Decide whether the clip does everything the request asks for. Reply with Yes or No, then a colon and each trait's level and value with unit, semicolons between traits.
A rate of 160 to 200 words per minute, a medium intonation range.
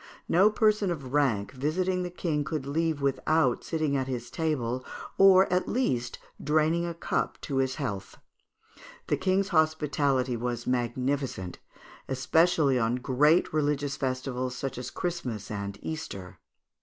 No: slow, 135 wpm; average, 4.5 semitones